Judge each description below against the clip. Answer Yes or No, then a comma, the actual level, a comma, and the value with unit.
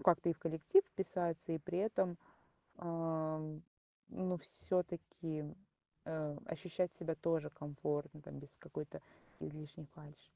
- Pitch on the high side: No, medium, 165 Hz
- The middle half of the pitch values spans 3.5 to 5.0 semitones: No, narrow, 2.5 semitones